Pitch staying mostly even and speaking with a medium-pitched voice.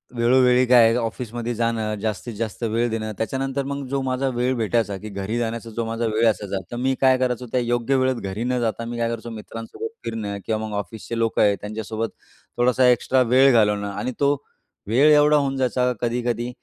No: narrow, 2.3 semitones; low, 115 Hz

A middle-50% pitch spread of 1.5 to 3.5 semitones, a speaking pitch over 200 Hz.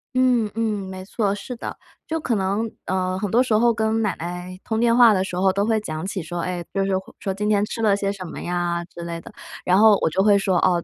No: average, 3.2 semitones; high, 195 Hz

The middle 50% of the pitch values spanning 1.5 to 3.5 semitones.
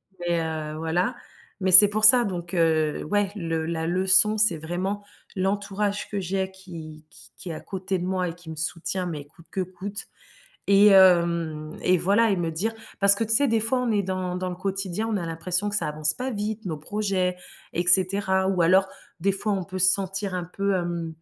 Yes: average, 2.9 semitones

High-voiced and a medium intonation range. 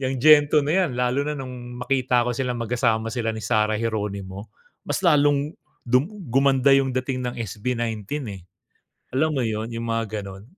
No: low, 125 Hz; average, 3.5 semitones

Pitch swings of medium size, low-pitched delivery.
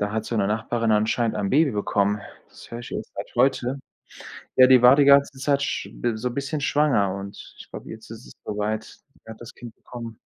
Yes: average, 3.7 semitones; low, 115 Hz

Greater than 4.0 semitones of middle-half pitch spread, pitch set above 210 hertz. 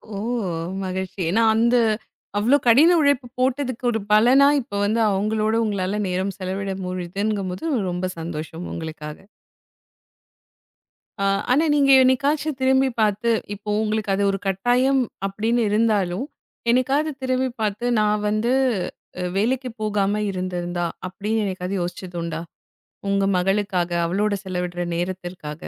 No: average, 4.7 semitones; high, 205 Hz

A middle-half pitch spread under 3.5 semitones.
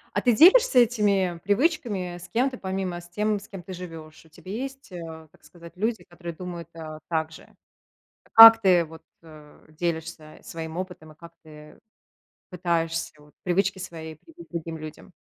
No: average, 3.8 semitones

